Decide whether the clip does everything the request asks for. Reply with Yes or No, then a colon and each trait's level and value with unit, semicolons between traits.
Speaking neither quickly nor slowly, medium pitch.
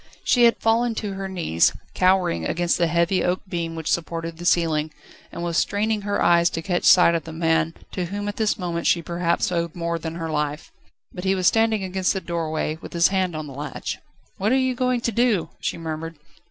No: fast, 220 wpm; medium, 175 Hz